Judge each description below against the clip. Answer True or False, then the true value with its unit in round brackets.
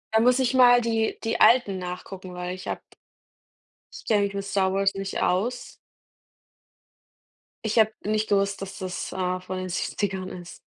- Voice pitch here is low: False (195 Hz)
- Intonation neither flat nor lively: True (3.1 semitones)